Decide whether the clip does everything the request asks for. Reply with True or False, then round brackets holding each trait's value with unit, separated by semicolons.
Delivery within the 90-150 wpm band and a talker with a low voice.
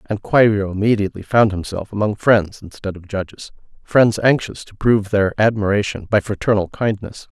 True (145 wpm; 105 Hz)